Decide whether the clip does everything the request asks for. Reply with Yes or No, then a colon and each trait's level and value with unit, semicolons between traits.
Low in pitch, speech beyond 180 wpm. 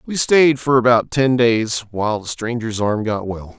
Yes: low, 115 Hz; average, 200 wpm